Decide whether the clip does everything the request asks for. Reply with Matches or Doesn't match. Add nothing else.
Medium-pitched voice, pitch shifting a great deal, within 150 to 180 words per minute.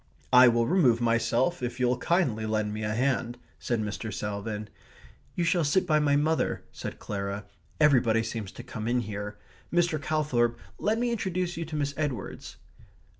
Doesn't match